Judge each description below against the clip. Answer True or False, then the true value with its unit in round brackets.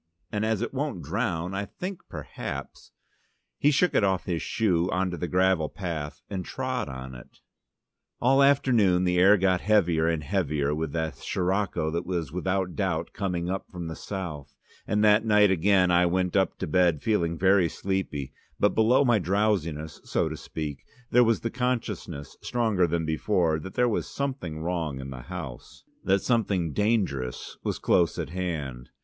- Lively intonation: False (4.3 semitones)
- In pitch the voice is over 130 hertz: False (90 Hz)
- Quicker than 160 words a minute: True (175 wpm)